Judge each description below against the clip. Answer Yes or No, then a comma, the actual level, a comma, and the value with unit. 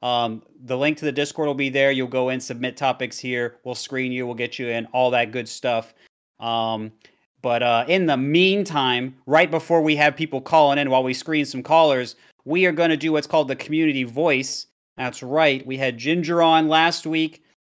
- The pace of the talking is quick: Yes, fast, 210 wpm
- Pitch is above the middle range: No, low, 135 Hz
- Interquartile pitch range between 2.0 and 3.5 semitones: No, average, 4.0 semitones